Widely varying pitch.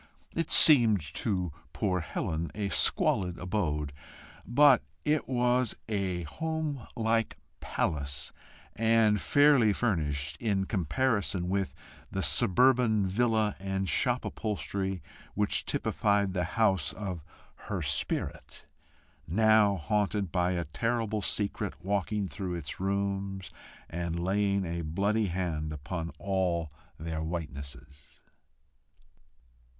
No: average, 4.3 semitones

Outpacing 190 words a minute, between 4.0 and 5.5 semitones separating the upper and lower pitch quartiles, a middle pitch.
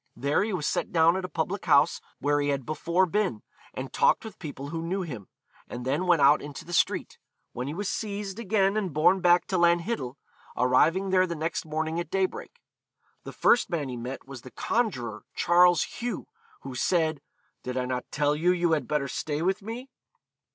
Yes: average, 200 wpm; average, 4.9 semitones; medium, 165 Hz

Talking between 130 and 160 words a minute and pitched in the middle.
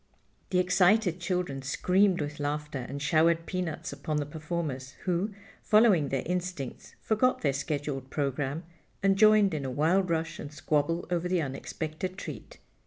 Yes: average, 150 wpm; medium, 165 Hz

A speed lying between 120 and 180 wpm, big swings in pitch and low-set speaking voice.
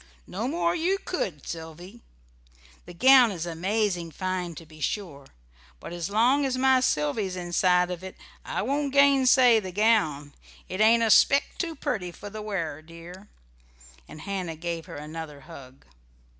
No: average, 155 wpm; wide, 6.4 semitones; medium, 185 Hz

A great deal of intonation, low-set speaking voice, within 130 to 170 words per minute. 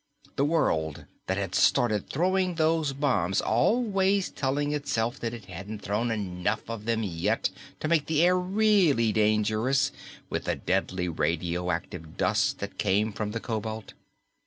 Yes: wide, 7.4 semitones; low, 110 Hz; average, 145 wpm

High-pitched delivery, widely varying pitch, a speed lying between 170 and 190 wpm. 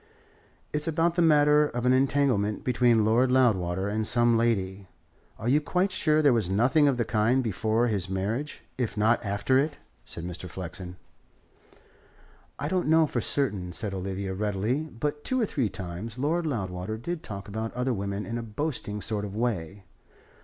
No: low, 115 Hz; wide, 6.0 semitones; average, 175 wpm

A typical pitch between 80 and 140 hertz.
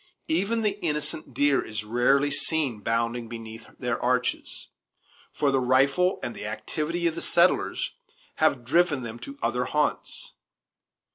Yes: low, 135 Hz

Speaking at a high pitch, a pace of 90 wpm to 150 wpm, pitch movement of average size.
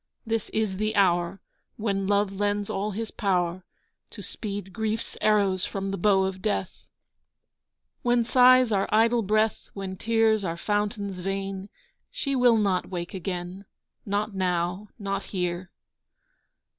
No: high, 200 Hz; slow, 135 wpm; narrow, 2.3 semitones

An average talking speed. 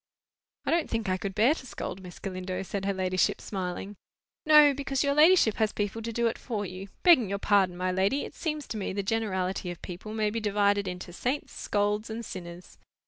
No: fast, 210 wpm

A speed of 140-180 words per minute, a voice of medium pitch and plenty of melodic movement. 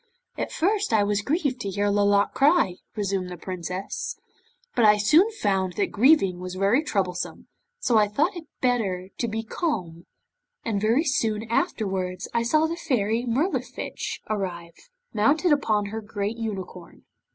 No: average, 150 wpm; high, 215 Hz; wide, 5.7 semitones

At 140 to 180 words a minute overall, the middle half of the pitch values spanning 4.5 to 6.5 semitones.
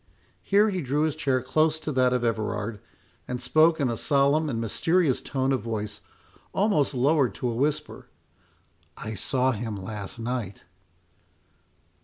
Yes: average, 145 wpm; average, 4.8 semitones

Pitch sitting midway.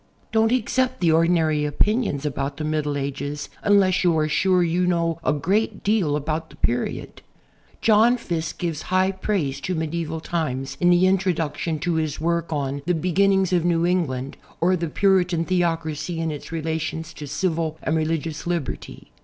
Yes: medium, 165 Hz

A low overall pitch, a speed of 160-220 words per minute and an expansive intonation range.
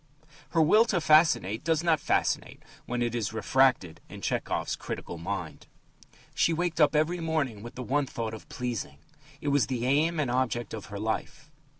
Yes: low, 130 Hz; average, 180 wpm; wide, 5.8 semitones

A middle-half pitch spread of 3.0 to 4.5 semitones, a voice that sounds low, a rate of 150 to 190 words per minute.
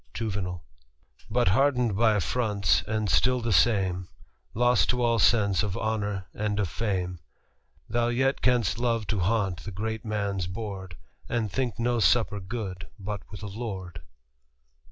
Yes: average, 3.5 semitones; low, 105 Hz; average, 155 wpm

